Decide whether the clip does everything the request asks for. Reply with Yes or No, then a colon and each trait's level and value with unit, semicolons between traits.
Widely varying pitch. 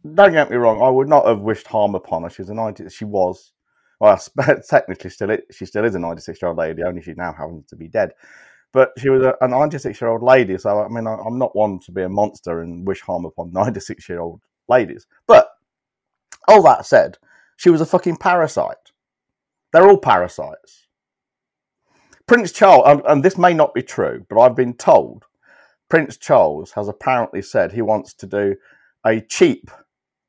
Yes: wide, 7.1 semitones